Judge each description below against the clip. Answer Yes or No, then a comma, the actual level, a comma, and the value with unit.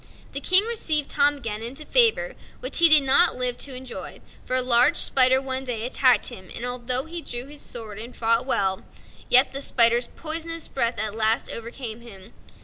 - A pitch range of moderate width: Yes, average, 3.9 semitones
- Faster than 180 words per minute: Yes, average, 190 wpm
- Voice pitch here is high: Yes, very high, 255 Hz